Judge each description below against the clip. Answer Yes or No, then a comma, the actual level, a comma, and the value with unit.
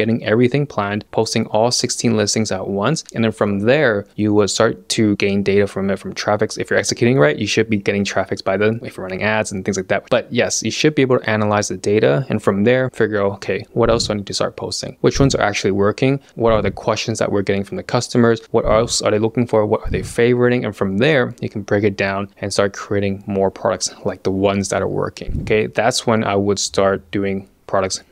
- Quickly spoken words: Yes, fast, 250 wpm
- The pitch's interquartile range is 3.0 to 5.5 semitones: No, narrow, 2.5 semitones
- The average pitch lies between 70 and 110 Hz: Yes, low, 105 Hz